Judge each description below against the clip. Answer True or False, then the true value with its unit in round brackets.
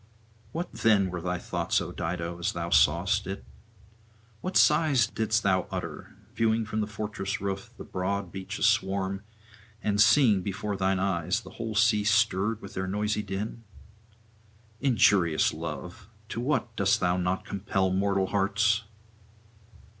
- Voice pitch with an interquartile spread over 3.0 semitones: False (2.6 semitones)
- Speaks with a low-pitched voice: True (100 Hz)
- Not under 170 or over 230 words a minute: False (145 wpm)